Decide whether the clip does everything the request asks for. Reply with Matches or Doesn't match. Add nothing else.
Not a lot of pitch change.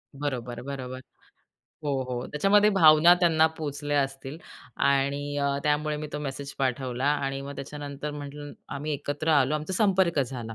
Matches